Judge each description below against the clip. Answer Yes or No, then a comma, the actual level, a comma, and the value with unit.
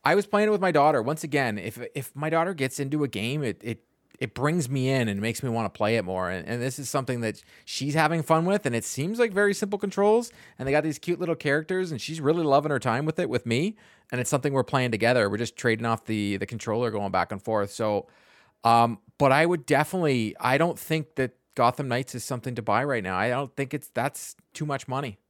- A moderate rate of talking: No, fast, 255 wpm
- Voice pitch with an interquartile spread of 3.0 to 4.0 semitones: No, average, 5.0 semitones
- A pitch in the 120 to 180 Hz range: Yes, low, 135 Hz